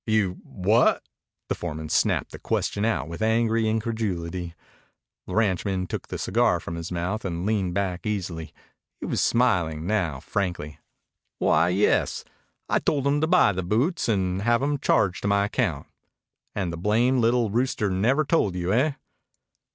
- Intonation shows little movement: No, average, 4.4 semitones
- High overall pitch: No, low, 100 Hz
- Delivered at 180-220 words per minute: No, average, 160 wpm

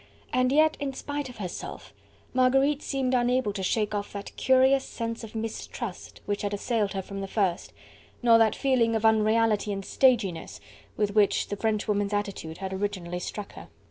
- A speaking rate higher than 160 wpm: Yes, average, 175 wpm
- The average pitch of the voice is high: Yes, high, 220 Hz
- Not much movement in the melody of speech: No, average, 3.9 semitones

